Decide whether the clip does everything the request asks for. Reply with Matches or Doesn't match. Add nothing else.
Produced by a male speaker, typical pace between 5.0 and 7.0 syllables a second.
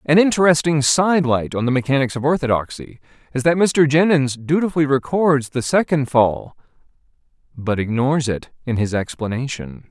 Matches